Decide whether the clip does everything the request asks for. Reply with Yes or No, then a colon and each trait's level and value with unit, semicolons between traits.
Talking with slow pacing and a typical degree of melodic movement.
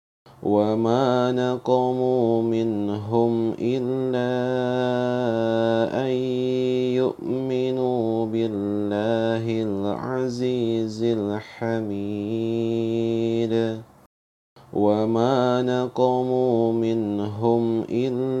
No: slow, 40 wpm; narrow, 1.9 semitones